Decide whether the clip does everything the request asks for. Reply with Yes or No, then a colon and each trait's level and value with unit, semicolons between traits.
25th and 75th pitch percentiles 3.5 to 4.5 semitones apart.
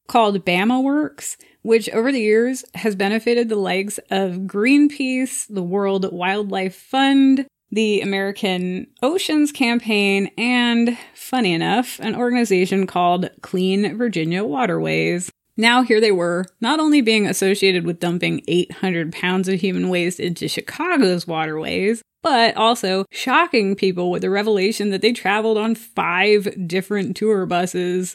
Yes: average, 4.2 semitones